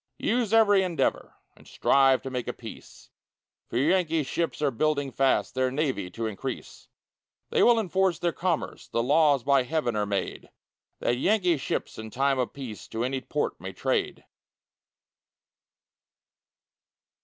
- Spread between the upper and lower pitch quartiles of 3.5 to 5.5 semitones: Yes, average, 5.2 semitones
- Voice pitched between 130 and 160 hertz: Yes, medium, 140 Hz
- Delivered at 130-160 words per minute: Yes, average, 145 wpm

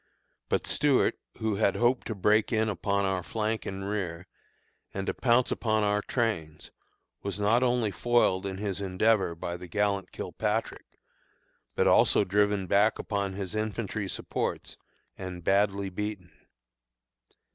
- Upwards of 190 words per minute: No, average, 140 wpm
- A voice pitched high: No, low, 100 Hz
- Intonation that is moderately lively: No, narrow, 2.3 semitones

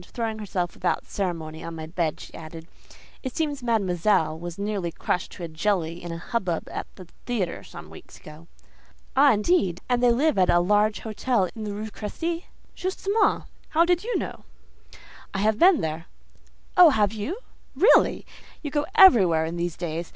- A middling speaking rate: Yes, average, 175 wpm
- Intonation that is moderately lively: No, wide, 6.5 semitones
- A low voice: No, high, 205 Hz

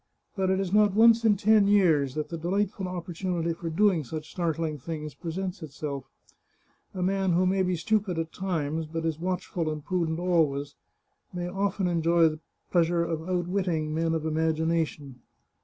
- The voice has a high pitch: No, medium, 170 Hz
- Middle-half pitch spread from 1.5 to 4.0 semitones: Yes, average, 2.8 semitones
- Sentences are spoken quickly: No, average, 170 wpm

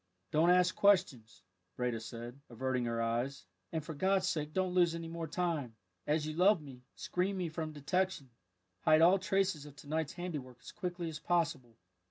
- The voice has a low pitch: No, medium, 160 Hz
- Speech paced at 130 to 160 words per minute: No, average, 180 wpm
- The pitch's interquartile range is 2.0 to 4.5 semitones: No, average, 5.2 semitones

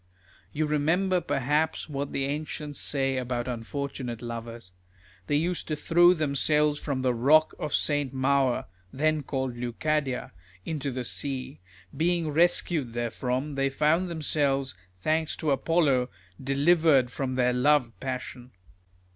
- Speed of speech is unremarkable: No, slow, 130 wpm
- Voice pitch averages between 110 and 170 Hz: Yes, medium, 140 Hz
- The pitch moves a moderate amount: Yes, average, 3.2 semitones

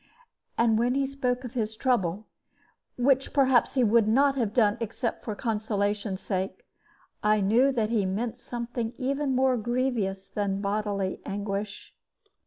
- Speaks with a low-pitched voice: No, high, 225 Hz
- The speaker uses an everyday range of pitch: Yes, average, 3.7 semitones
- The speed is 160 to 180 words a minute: No, average, 150 wpm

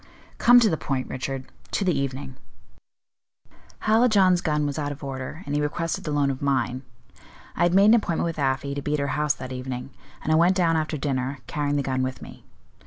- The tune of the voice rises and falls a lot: No, average, 3.8 semitones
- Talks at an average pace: No, fast, 215 wpm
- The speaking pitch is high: No, medium, 145 Hz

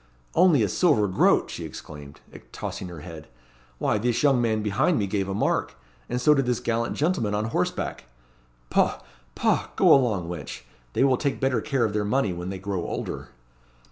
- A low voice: Yes, low, 110 Hz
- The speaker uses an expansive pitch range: Yes, wide, 5.7 semitones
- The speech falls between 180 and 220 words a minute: Yes, average, 185 wpm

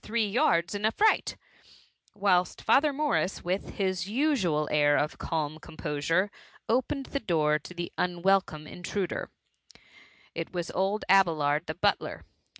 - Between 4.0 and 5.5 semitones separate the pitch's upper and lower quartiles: Yes, average, 4.8 semitones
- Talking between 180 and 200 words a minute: No, average, 145 wpm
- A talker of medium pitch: Yes, medium, 180 Hz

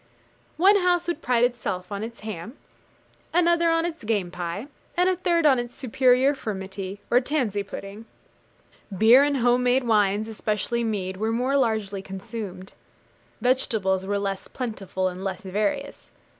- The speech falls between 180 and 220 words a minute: No, average, 150 wpm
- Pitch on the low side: No, high, 225 Hz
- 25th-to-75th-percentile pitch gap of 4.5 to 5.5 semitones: Yes, average, 5.2 semitones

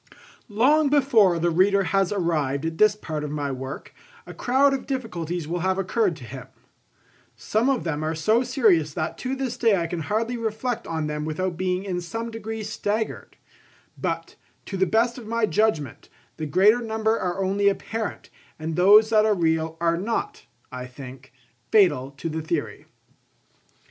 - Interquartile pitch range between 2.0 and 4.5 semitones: No, wide, 5.6 semitones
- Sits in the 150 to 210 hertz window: Yes, high, 190 Hz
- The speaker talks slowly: No, average, 175 wpm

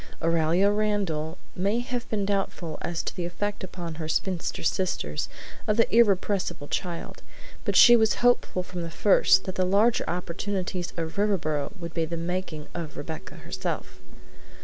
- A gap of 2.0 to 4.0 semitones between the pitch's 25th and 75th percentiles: Yes, average, 3.6 semitones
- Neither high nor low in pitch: Yes, medium, 180 Hz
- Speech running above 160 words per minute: No, average, 155 wpm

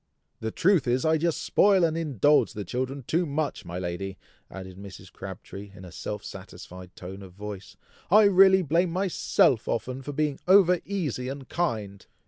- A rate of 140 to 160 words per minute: No, average, 170 wpm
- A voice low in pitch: Yes, low, 130 Hz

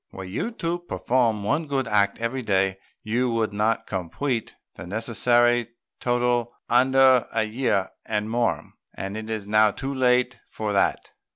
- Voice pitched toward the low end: Yes, low, 115 Hz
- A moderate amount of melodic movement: Yes, average, 3.0 semitones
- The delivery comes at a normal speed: Yes, average, 155 wpm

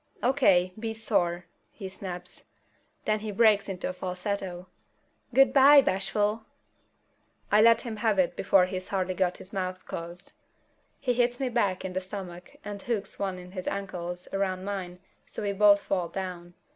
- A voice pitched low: No, high, 195 Hz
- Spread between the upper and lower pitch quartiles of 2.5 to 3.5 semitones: Yes, average, 2.8 semitones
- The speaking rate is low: No, average, 160 wpm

